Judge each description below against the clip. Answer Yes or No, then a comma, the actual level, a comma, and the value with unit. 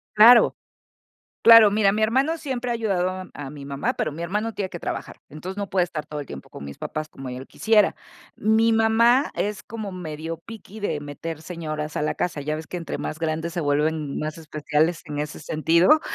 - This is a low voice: No, medium, 170 Hz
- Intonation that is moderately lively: No, wide, 5.9 semitones